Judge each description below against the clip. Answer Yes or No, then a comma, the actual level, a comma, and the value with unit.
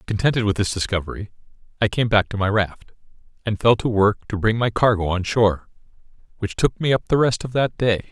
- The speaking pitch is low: Yes, low, 105 Hz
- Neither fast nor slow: No, fast, 215 wpm